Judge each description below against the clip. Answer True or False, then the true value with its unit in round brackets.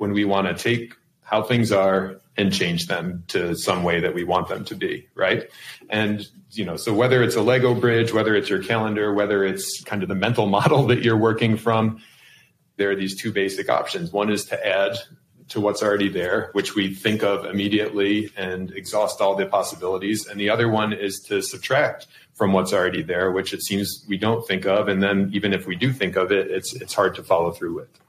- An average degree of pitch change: False (2.3 semitones)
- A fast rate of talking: True (220 wpm)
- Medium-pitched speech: False (105 Hz)